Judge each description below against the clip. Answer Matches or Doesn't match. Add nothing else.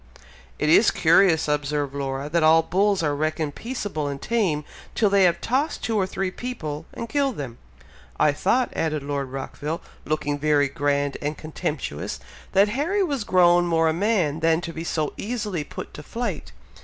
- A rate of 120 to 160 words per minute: Doesn't match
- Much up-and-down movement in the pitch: Matches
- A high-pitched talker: Doesn't match